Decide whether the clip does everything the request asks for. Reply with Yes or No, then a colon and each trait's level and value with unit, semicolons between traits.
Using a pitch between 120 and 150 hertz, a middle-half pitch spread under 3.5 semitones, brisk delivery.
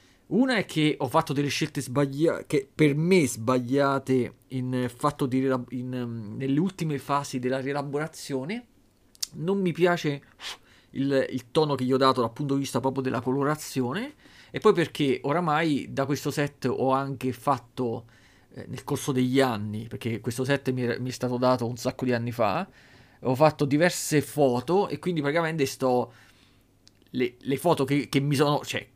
Yes: low, 135 Hz; narrow, 2.4 semitones; fast, 175 wpm